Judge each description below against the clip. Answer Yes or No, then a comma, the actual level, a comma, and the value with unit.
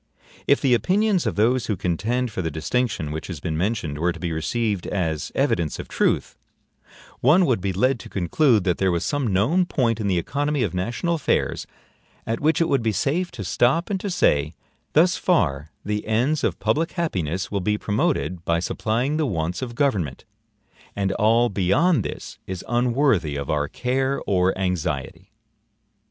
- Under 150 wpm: No, average, 180 wpm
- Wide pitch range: Yes, wide, 7.5 semitones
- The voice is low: Yes, low, 110 Hz